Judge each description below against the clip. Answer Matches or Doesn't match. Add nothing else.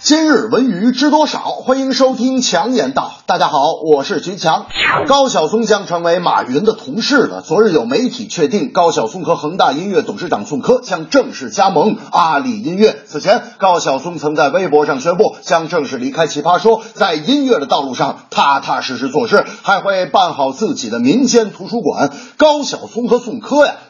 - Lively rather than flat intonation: Matches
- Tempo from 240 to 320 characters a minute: Matches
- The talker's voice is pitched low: Doesn't match